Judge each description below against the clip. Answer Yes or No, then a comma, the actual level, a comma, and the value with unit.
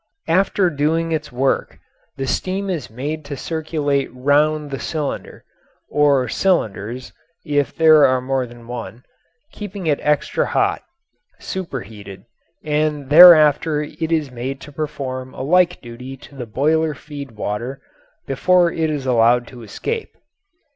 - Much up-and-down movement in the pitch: No, average, 3.7 semitones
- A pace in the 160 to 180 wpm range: No, slow, 135 wpm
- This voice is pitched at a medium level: Yes, medium, 145 Hz